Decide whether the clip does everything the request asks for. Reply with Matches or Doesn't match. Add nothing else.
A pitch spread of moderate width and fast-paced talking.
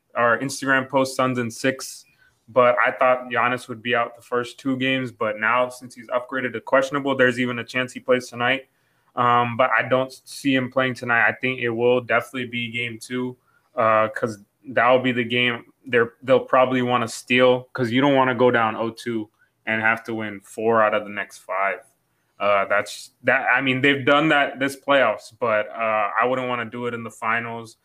Doesn't match